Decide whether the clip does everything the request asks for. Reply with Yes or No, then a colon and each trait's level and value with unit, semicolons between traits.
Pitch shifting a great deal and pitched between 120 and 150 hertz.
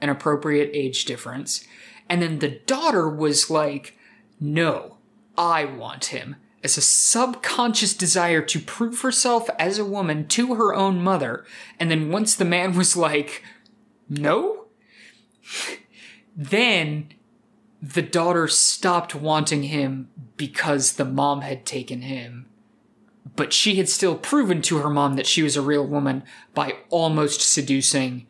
No: wide, 6.4 semitones; medium, 160 Hz